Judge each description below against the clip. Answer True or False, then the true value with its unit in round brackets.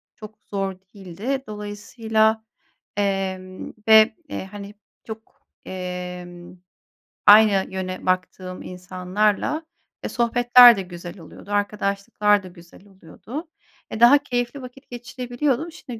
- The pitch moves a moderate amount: True (4.2 semitones)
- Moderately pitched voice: False (205 Hz)